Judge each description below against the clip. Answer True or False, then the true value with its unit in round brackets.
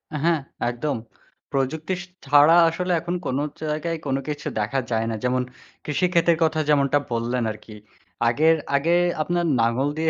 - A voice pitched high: False (145 Hz)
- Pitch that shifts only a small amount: False (4.3 semitones)